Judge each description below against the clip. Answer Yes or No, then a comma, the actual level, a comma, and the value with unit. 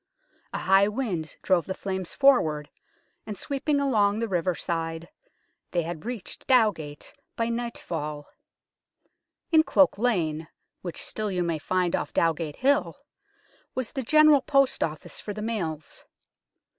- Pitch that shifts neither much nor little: No, wide, 6.9 semitones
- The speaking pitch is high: Yes, high, 195 Hz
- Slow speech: Yes, slow, 130 wpm